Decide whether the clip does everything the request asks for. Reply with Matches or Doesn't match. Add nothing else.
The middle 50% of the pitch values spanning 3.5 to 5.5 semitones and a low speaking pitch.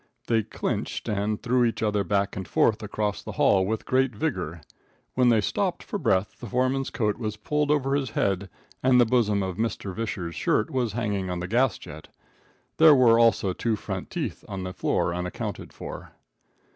Matches